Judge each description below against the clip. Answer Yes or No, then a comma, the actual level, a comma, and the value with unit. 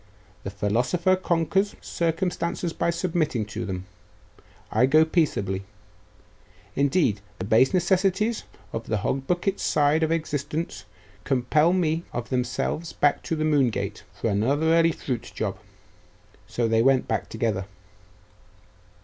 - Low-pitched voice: No, medium, 150 Hz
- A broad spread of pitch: Yes, wide, 6.4 semitones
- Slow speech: Yes, slow, 130 wpm